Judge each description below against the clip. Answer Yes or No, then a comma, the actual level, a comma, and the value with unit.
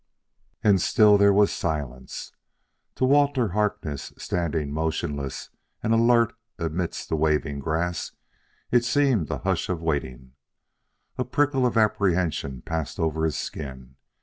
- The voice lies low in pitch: Yes, very low, 85 Hz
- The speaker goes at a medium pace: No, slow, 125 wpm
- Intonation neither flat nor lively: No, wide, 6.6 semitones